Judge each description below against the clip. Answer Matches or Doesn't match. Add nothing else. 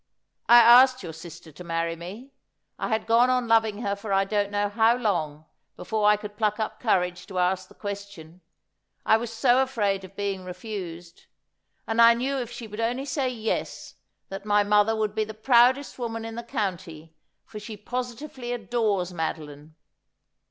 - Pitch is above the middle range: Matches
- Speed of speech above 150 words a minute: Matches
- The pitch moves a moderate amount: Matches